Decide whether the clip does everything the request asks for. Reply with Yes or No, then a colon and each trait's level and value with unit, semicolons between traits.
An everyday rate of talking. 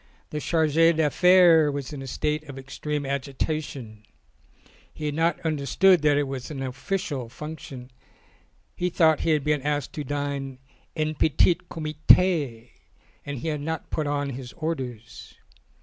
Yes: average, 155 wpm